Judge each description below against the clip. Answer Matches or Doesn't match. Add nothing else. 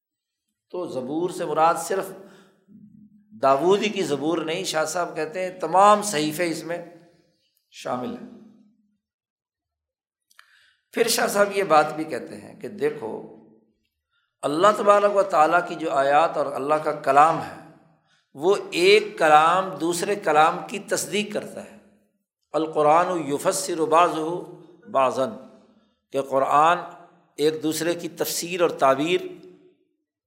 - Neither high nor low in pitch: Matches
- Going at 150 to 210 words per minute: Doesn't match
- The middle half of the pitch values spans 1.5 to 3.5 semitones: Doesn't match